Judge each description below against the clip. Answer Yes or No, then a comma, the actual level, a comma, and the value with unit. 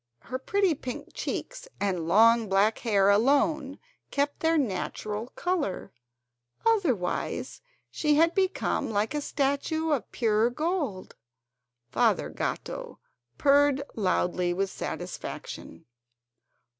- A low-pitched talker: No, very high, 260 Hz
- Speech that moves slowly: Yes, slow, 105 wpm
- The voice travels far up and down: Yes, wide, 7.1 semitones